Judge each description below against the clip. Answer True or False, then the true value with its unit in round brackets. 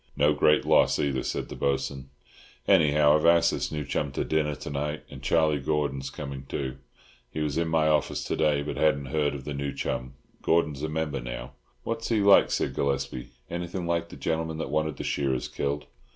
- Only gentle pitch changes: True (2.2 semitones)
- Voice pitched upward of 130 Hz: False (75 Hz)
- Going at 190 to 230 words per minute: True (200 wpm)